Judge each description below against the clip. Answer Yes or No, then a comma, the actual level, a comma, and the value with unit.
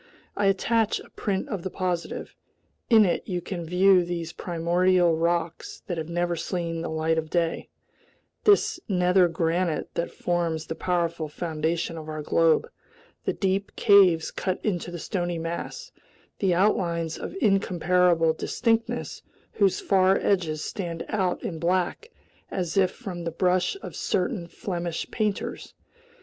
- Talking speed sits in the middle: Yes, average, 145 wpm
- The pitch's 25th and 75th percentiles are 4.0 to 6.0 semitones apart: No, narrow, 2.4 semitones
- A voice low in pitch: No, medium, 175 Hz